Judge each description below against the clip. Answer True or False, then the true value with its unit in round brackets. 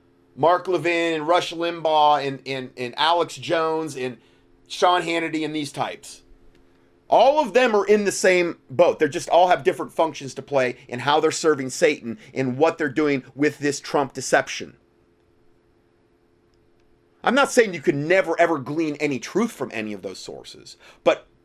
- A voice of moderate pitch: True (145 Hz)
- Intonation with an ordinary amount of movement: False (7.6 semitones)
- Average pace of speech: True (170 wpm)